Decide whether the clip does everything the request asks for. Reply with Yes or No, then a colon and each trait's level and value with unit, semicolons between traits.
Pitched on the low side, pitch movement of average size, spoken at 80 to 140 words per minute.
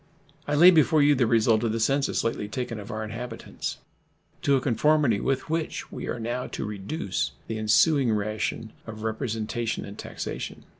No: low, 115 Hz; average, 4.2 semitones; average, 170 wpm